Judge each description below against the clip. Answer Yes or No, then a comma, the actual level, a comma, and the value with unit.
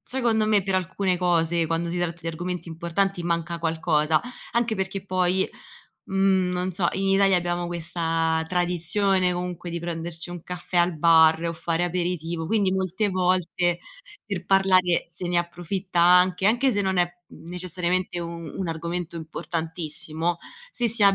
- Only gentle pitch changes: Yes, narrow, 2.0 semitones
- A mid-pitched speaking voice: Yes, medium, 175 Hz